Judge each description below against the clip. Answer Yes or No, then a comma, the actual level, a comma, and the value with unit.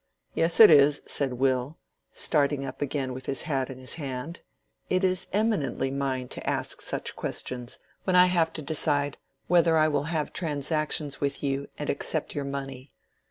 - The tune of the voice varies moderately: Yes, average, 3.0 semitones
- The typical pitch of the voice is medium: Yes, medium, 145 Hz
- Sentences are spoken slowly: No, average, 170 wpm